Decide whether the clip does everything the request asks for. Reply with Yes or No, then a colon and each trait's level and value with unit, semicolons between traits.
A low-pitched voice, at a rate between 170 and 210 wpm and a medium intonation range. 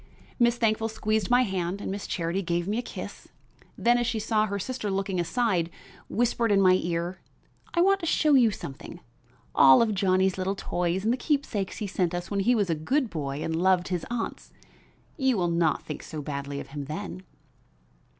No: high, 195 Hz; average, 200 wpm; average, 4.9 semitones